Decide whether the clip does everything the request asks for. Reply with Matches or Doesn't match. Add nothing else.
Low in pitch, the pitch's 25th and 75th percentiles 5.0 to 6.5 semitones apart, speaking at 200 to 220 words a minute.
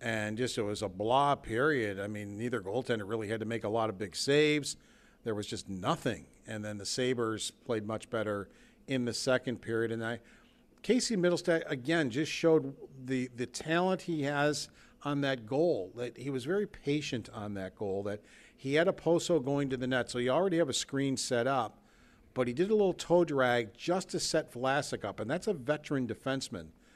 Matches